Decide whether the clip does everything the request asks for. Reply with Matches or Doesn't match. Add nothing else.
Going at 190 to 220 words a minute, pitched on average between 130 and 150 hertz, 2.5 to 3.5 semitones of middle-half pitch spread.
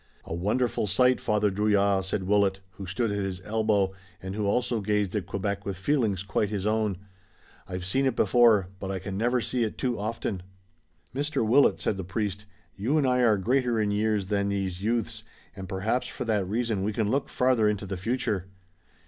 Doesn't match